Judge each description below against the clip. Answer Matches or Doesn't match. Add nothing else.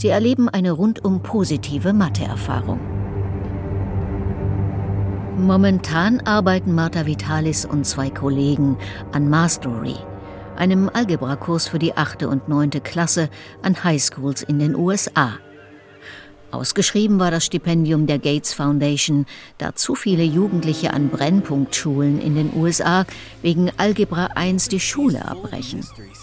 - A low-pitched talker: Doesn't match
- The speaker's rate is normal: Doesn't match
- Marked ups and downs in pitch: Matches